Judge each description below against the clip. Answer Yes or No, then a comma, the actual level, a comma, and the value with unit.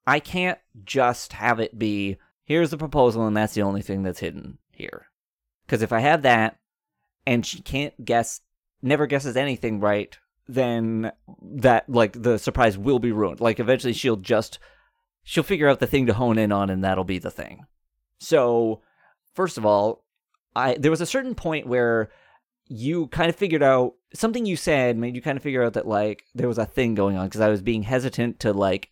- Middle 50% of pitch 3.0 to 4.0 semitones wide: No, average, 4.8 semitones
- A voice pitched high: No, low, 120 Hz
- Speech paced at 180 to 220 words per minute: Yes, average, 200 wpm